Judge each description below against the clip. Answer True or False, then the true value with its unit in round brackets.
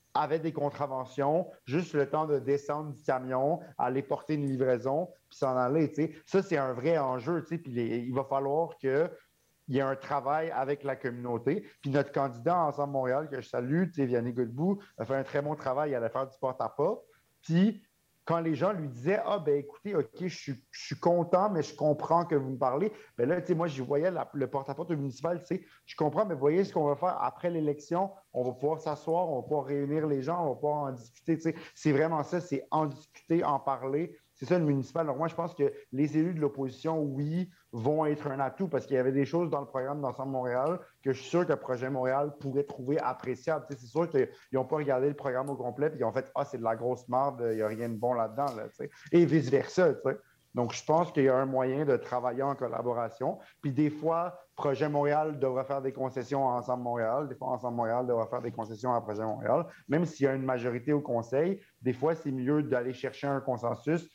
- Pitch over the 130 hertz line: True (140 Hz)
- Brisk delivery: True (240 wpm)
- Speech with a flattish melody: False (3.7 semitones)